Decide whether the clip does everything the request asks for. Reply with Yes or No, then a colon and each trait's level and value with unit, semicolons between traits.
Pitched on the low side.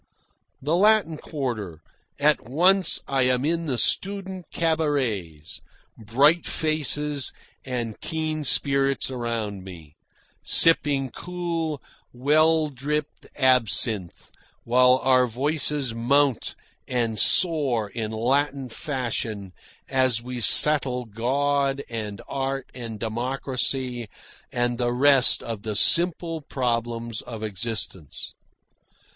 Yes: low, 130 Hz